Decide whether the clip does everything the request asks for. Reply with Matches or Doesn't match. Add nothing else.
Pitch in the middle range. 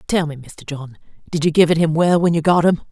Matches